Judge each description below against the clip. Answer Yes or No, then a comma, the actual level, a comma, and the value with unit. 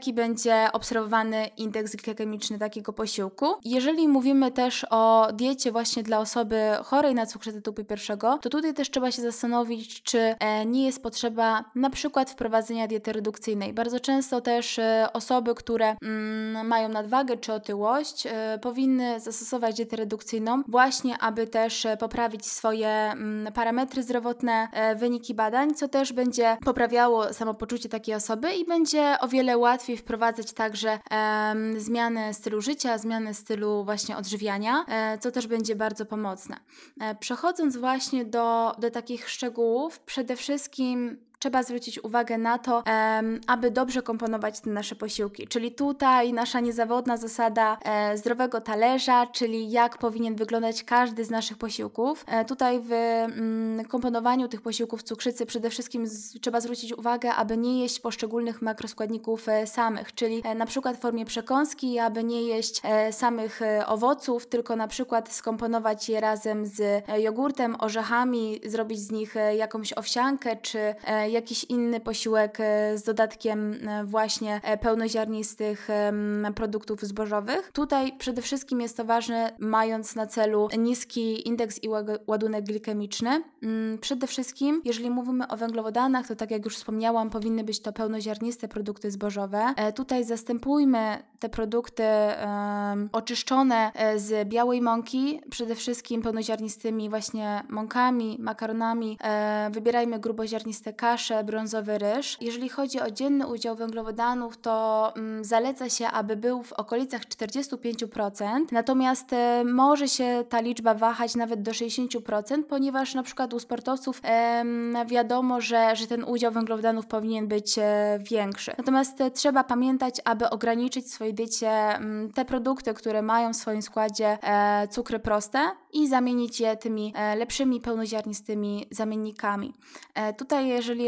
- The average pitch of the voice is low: No, high, 230 Hz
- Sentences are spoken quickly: No, average, 130 wpm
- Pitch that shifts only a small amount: Yes, narrow, 2.0 semitones